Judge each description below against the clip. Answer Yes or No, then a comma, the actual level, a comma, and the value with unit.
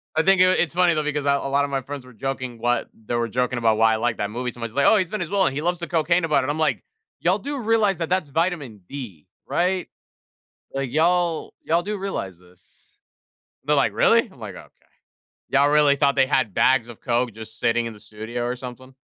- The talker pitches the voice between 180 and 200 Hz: No, medium, 140 Hz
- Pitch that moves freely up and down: Yes, wide, 6.1 semitones